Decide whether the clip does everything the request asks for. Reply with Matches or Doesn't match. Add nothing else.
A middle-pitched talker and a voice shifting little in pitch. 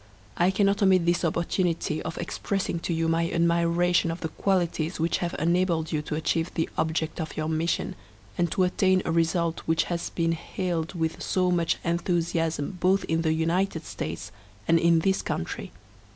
Matches